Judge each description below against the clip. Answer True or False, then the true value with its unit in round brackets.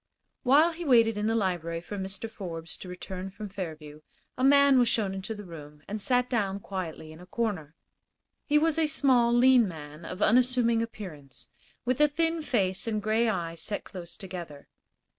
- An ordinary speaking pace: True (180 wpm)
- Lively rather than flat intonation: True (5.8 semitones)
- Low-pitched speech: False (205 Hz)